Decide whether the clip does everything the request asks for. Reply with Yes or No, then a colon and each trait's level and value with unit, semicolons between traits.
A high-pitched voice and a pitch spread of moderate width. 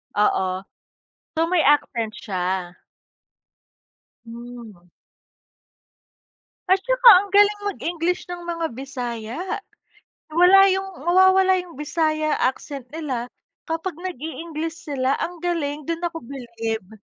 No: very high, 310 Hz; wide, 6.8 semitones